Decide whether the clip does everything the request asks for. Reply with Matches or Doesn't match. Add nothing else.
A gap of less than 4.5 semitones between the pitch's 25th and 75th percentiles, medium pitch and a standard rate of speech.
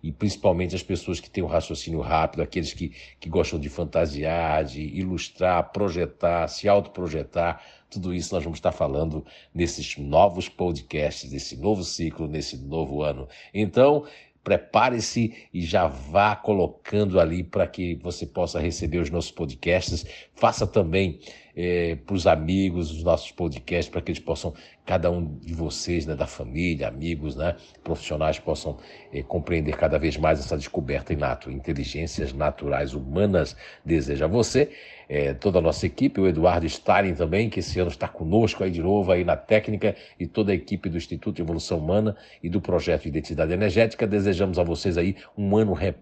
Doesn't match